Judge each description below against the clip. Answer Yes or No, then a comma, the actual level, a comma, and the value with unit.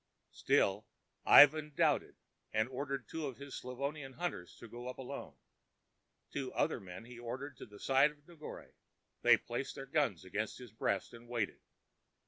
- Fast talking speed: No, average, 160 wpm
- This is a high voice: No, low, 130 Hz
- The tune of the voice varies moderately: Yes, average, 3.6 semitones